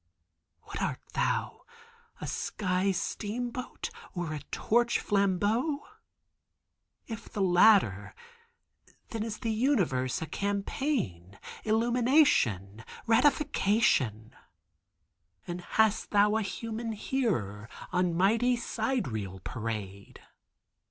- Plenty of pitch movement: Yes, wide, 7.9 semitones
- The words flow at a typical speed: No, slow, 85 wpm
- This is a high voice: Yes, high, 205 Hz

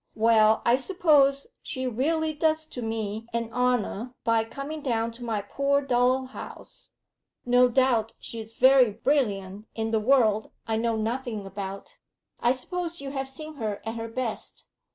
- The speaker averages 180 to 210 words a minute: No, average, 155 wpm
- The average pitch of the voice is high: Yes, high, 245 Hz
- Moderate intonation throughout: Yes, average, 3.5 semitones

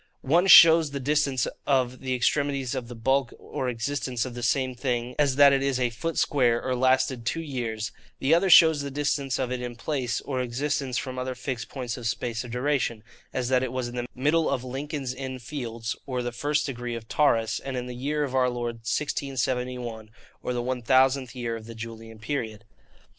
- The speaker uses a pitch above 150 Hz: No, low, 130 Hz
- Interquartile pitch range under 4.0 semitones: Yes, narrow, 2.5 semitones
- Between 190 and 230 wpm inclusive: Yes, fast, 205 wpm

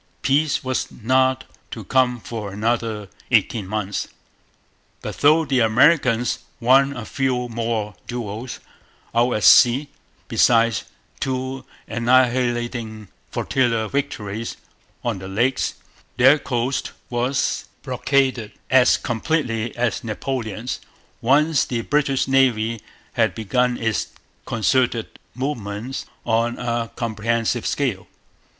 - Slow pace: Yes, slow, 105 wpm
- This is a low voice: Yes, low, 120 Hz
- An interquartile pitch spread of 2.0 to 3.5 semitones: Yes, narrow, 2.6 semitones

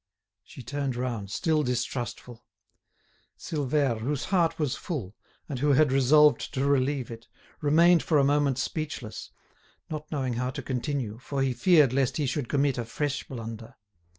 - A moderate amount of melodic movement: Yes, average, 3.2 semitones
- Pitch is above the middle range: No, low, 135 Hz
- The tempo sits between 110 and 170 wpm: Yes, average, 155 wpm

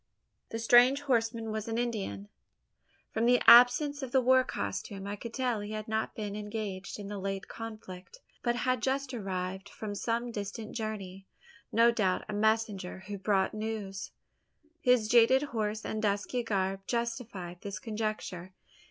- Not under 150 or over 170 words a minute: Yes, average, 155 wpm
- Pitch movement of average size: Yes, average, 3.1 semitones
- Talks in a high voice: Yes, high, 220 Hz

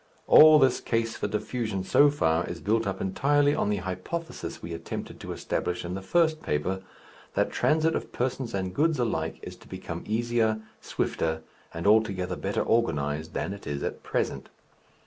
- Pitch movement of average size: No, wide, 5.9 semitones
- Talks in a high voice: No, low, 105 Hz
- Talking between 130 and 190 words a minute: Yes, average, 170 wpm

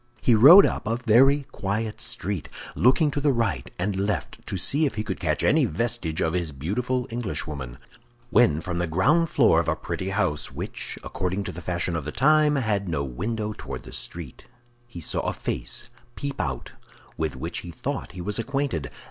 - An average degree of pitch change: No, wide, 7.0 semitones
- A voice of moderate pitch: No, low, 100 Hz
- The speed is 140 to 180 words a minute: No, average, 195 wpm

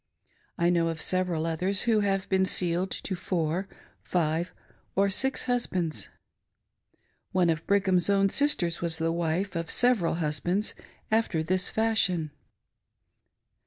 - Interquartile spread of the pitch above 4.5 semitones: No, average, 3.0 semitones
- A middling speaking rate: No, slow, 125 wpm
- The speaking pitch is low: No, medium, 180 Hz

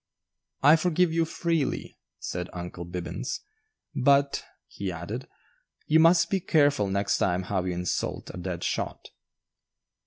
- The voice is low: Yes, low, 125 Hz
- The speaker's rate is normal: No, slow, 130 wpm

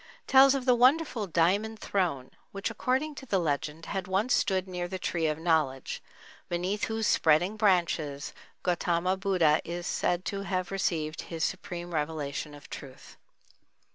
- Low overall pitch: No, medium, 180 Hz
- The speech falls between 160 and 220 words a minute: No, average, 150 wpm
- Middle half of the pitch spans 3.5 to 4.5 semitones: Yes, average, 4.0 semitones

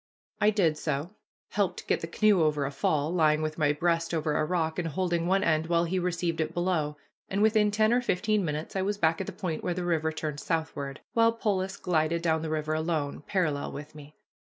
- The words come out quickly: Yes, fast, 220 wpm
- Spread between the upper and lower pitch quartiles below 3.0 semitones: No, average, 3.3 semitones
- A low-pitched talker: No, medium, 165 Hz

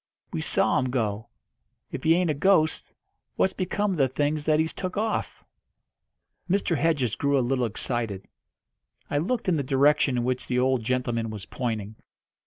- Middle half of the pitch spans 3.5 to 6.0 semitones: Yes, average, 5.0 semitones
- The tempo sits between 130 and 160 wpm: No, average, 175 wpm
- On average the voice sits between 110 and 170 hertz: Yes, low, 135 Hz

